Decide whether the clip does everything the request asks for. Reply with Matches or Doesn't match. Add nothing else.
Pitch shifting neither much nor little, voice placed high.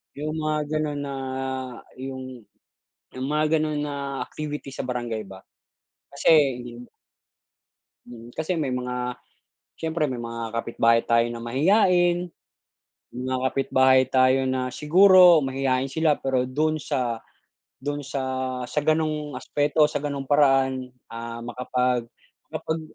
Doesn't match